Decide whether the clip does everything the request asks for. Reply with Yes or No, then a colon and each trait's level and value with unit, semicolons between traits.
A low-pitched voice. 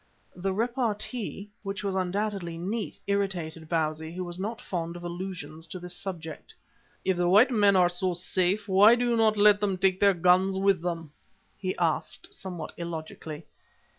No: medium, 185 Hz